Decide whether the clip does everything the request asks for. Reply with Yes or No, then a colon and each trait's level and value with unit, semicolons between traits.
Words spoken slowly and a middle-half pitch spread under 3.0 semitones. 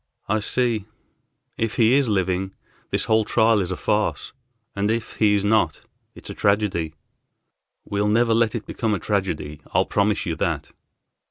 No: average, 165 wpm; narrow, 2.4 semitones